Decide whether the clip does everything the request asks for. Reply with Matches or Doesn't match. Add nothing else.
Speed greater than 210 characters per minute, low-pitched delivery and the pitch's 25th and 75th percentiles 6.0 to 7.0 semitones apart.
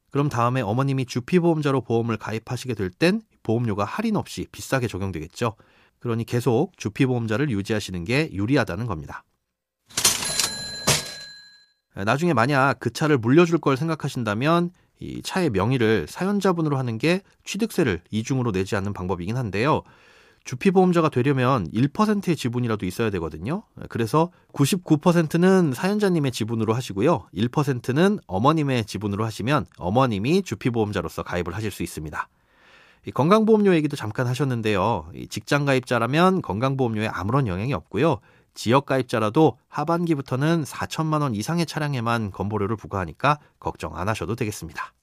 Matches